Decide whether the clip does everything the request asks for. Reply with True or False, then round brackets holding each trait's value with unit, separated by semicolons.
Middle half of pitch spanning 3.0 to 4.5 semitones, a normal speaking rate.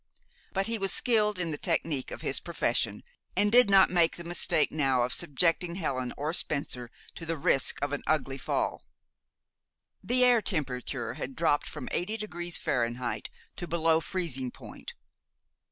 False (5.5 semitones; 160 wpm)